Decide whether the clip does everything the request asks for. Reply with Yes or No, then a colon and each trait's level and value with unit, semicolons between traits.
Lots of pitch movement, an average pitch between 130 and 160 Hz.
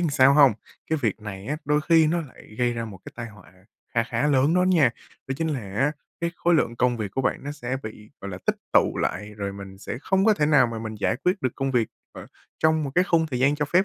Yes: wide, 5.7 semitones; low, 135 Hz